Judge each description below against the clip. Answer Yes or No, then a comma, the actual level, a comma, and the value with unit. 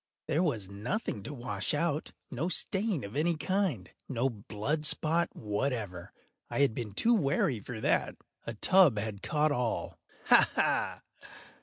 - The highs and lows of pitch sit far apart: Yes, wide, 7.0 semitones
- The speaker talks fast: No, slow, 135 wpm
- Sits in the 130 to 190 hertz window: Yes, low, 135 Hz